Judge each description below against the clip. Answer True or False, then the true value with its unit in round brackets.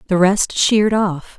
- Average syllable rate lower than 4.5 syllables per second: True (4.2 syllables/s)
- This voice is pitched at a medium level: False (195 Hz)